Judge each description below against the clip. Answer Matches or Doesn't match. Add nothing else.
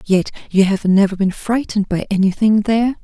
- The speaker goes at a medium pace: Matches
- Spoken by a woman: Matches